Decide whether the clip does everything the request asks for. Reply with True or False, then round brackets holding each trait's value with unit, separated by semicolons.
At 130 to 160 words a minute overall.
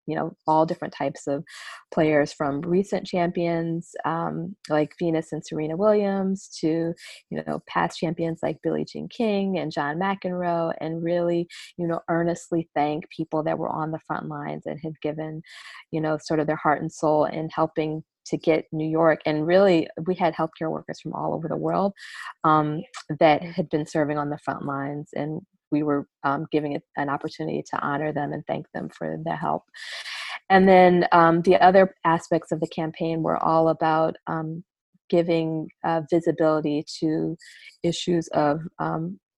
False (175 wpm)